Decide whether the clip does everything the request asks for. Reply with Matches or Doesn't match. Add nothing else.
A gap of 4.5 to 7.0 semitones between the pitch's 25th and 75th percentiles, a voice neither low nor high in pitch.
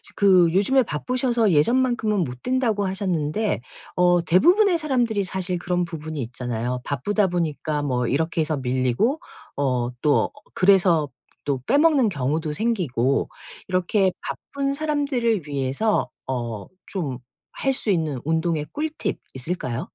Doesn't match